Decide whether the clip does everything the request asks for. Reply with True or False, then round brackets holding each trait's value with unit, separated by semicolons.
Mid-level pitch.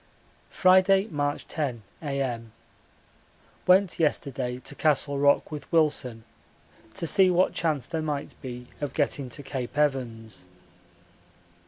True (145 Hz)